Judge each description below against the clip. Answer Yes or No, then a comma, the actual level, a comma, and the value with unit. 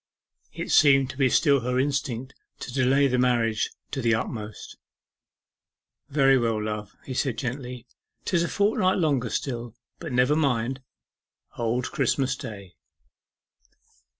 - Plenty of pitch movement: No, average, 2.9 semitones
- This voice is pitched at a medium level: No, low, 130 Hz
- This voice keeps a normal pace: No, slow, 130 wpm